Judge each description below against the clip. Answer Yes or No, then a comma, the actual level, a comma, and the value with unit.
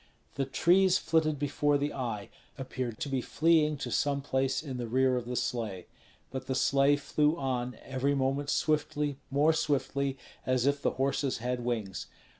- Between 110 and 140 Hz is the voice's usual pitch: Yes, low, 135 Hz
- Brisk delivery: No, average, 170 wpm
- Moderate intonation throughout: No, narrow, 2.3 semitones